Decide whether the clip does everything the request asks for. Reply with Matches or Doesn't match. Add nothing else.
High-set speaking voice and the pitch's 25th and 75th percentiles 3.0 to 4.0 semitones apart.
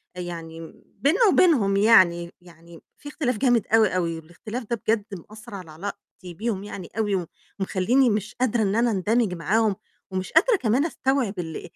Doesn't match